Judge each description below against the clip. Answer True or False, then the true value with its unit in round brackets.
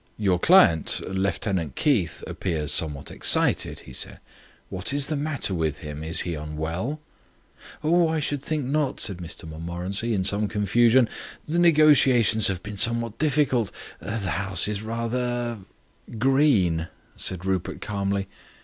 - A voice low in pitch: True (105 Hz)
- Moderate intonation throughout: False (7.0 semitones)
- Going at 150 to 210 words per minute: False (140 wpm)